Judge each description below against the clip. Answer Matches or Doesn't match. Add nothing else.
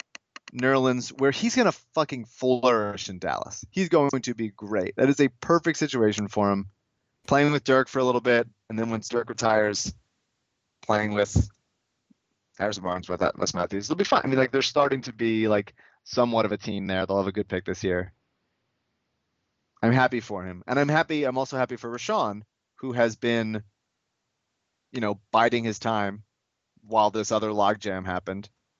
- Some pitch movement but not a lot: Matches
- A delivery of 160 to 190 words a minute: Matches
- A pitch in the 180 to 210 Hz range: Doesn't match